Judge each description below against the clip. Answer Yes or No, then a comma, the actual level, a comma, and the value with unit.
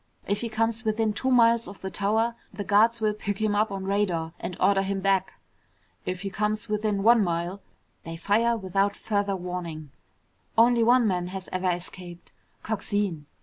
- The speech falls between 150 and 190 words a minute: Yes, average, 175 wpm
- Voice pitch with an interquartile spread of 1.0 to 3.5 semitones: Yes, average, 2.9 semitones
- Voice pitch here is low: No, high, 200 Hz